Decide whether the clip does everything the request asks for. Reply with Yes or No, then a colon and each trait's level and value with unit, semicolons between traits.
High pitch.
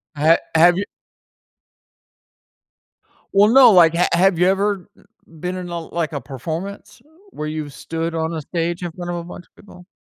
No: medium, 175 Hz